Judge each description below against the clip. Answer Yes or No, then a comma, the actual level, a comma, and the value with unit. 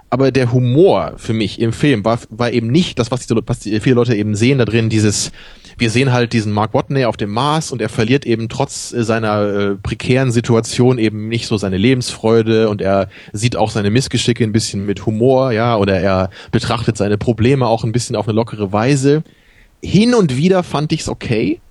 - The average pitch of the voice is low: Yes, low, 115 Hz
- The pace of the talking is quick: Yes, fast, 205 wpm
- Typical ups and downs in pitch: Yes, average, 3.3 semitones